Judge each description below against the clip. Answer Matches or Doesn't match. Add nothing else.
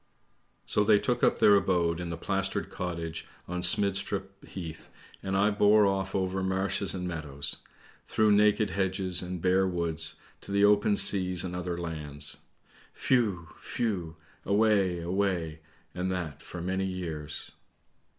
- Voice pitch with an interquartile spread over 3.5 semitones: Doesn't match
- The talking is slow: Doesn't match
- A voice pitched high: Doesn't match